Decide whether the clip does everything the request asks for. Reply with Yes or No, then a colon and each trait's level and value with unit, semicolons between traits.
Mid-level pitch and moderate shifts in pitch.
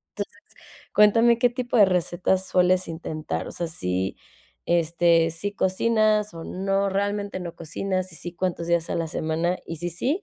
Yes: medium, 180 Hz; average, 3.3 semitones